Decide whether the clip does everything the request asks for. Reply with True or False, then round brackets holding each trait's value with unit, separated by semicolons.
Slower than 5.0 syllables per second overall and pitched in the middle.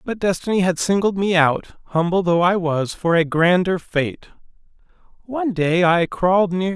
True (4.7 syllables/s; 180 Hz)